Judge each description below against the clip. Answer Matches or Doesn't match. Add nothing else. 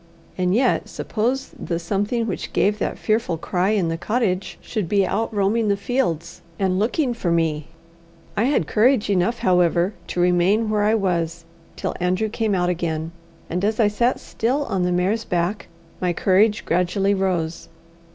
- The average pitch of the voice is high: Matches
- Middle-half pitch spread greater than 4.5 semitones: Doesn't match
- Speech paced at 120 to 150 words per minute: Doesn't match